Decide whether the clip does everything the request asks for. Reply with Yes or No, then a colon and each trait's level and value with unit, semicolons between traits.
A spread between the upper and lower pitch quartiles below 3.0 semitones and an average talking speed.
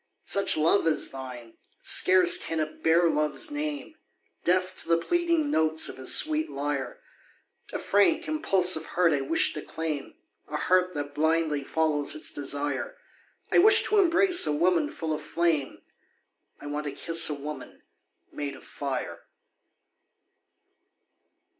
No: average, 4.2 semitones; average, 145 wpm